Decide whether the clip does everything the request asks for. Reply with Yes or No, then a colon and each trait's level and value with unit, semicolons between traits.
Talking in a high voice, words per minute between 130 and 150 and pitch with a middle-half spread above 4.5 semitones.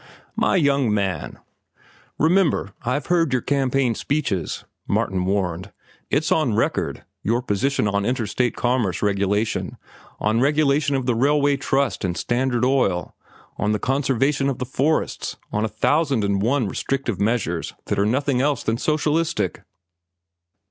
No: low, 125 Hz; average, 140 wpm; average, 5.3 semitones